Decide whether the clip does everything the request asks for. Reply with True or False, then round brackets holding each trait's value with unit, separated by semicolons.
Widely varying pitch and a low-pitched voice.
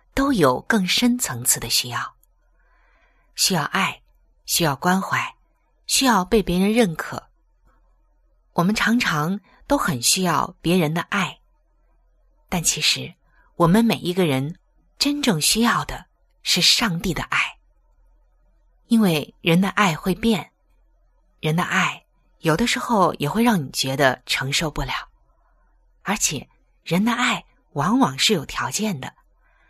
False (7.1 semitones; 180 Hz)